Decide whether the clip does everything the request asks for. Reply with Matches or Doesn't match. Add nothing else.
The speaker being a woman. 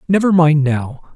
Doesn't match